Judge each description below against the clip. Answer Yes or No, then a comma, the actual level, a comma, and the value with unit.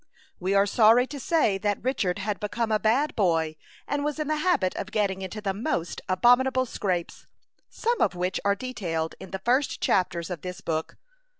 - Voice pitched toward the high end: Yes, high, 205 Hz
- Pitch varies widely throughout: Yes, wide, 5.7 semitones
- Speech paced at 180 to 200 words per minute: Yes, average, 190 wpm